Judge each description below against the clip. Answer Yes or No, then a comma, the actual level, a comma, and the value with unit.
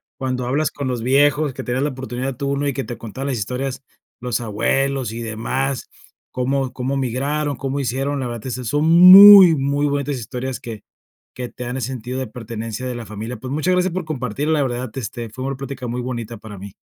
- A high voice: No, low, 130 Hz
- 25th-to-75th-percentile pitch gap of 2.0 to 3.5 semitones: Yes, narrow, 2.5 semitones